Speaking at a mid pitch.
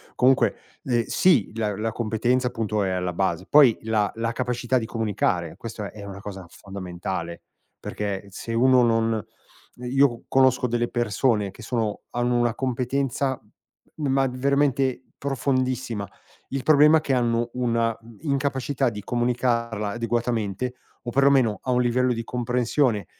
No: low, 120 Hz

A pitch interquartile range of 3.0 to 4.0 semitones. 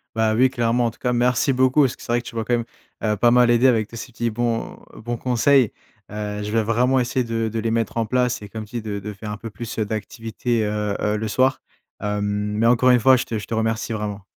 No: narrow, 2.4 semitones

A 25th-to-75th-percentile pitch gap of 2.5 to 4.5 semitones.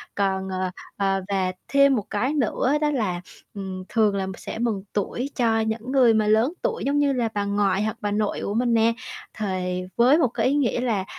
Yes: average, 4.0 semitones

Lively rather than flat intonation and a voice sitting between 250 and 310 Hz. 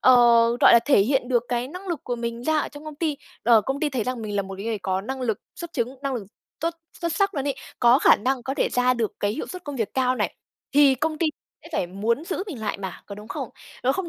No: average, 4.5 semitones; very high, 255 Hz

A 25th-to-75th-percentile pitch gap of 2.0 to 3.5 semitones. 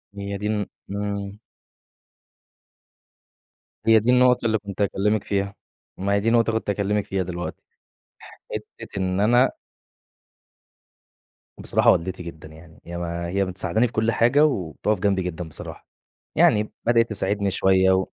Yes: average, 2.7 semitones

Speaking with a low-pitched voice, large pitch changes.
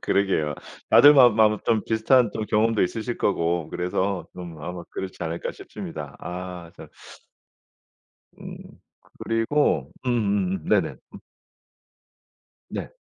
No: low, 100 Hz; average, 4.4 semitones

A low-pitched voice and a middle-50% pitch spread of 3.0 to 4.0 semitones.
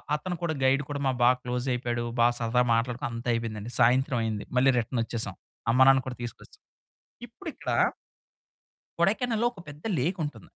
Yes: low, 125 Hz; average, 3.6 semitones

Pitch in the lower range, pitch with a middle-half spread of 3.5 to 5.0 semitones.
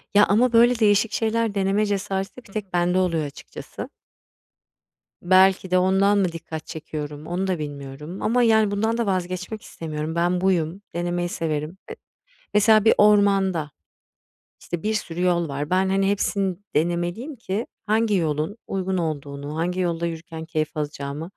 No: medium, 185 Hz; average, 3.9 semitones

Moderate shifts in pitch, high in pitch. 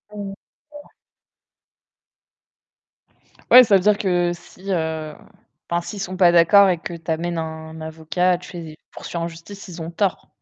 No: average, 3.0 semitones; medium, 175 Hz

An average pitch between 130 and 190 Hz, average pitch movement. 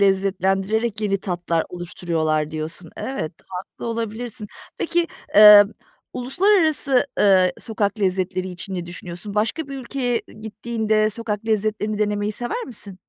No: high, 210 Hz; average, 3.8 semitones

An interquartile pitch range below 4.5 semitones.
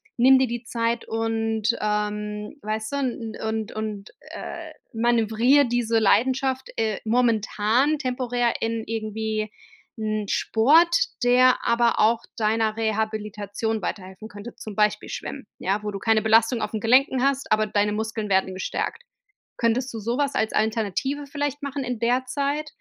Yes: average, 2.7 semitones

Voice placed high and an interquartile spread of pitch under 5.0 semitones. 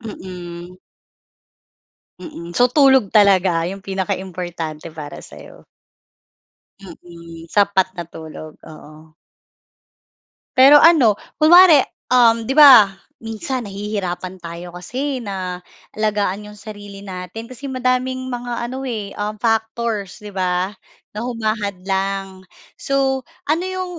No: high, 205 Hz; average, 5.3 semitones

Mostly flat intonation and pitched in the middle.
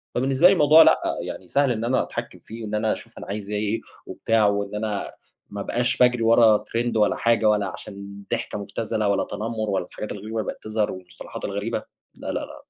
No: narrow, 2.3 semitones; low, 110 Hz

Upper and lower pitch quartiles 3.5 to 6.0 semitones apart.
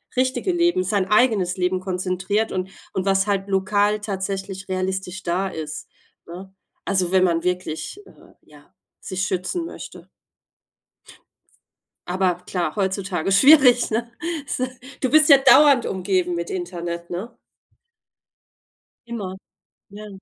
No: average, 2.7 semitones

